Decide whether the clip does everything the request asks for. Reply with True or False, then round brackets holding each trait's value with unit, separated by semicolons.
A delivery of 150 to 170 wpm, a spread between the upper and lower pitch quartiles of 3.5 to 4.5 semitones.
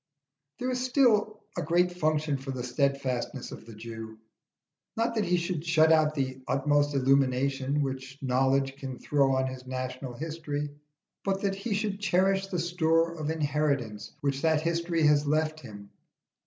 True (160 wpm; 4.1 semitones)